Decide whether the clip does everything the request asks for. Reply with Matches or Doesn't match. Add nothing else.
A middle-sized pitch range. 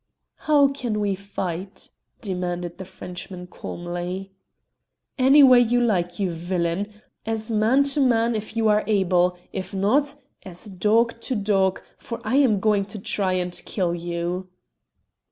Matches